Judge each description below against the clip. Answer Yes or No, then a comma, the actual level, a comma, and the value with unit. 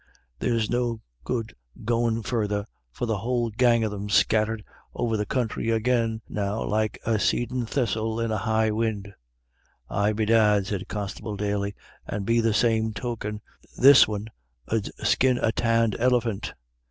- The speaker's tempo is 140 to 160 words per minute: Yes, average, 150 wpm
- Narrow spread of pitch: Yes, narrow, 1.8 semitones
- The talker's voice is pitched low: Yes, low, 110 Hz